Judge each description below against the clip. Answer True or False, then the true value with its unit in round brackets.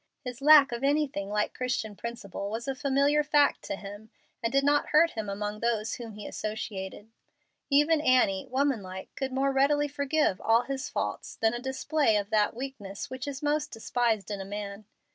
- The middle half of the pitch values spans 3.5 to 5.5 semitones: True (5.0 semitones)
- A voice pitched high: True (245 Hz)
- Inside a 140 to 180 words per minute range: False (190 wpm)